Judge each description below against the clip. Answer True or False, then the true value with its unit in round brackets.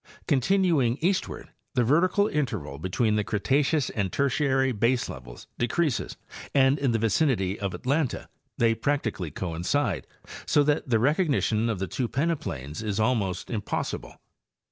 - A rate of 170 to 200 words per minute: False (135 wpm)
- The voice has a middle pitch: False (120 Hz)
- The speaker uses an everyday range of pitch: False (6.0 semitones)